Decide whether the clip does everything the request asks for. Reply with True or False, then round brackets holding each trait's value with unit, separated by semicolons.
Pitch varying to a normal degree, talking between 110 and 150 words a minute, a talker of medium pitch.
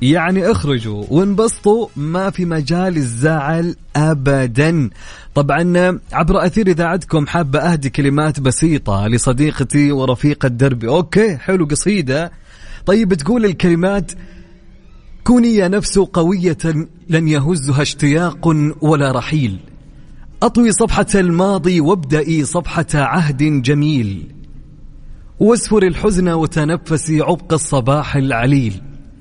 False (4.1 semitones; 95 wpm; 160 Hz)